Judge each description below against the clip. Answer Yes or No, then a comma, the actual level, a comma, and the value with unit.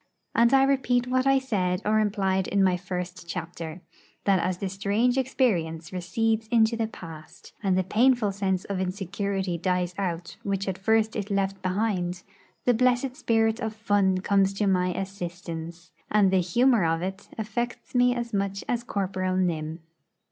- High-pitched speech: Yes, high, 195 Hz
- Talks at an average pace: Yes, average, 165 wpm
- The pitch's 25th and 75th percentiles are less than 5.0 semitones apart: Yes, average, 3.6 semitones